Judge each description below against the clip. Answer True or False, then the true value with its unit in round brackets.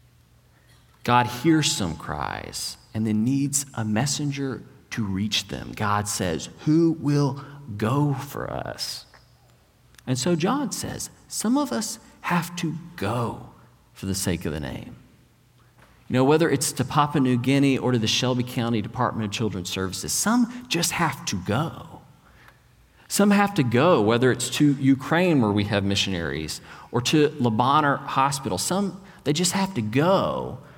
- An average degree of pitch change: False (5.8 semitones)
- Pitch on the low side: True (130 Hz)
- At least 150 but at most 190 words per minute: True (155 wpm)